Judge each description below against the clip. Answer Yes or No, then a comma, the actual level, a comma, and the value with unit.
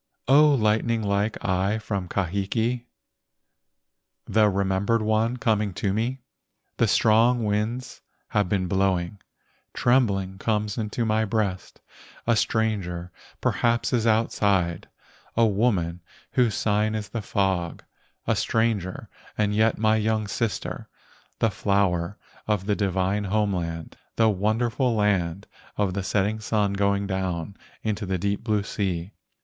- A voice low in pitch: Yes, low, 105 Hz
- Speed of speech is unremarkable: No, slow, 130 wpm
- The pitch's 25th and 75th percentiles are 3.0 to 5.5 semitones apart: No, narrow, 2.5 semitones